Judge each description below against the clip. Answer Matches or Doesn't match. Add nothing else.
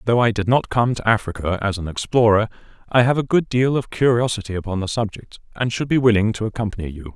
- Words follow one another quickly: Matches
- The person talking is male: Matches